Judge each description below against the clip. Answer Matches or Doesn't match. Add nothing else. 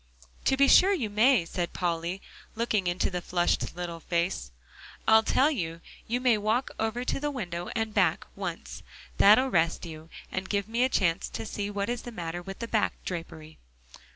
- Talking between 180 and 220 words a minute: Matches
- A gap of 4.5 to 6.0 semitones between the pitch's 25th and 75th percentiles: Matches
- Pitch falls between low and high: Doesn't match